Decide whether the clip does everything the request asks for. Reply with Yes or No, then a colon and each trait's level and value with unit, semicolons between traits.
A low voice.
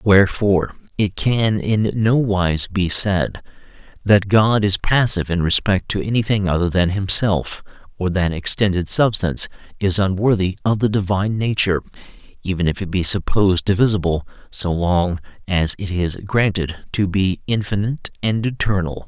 Yes: very low, 95 Hz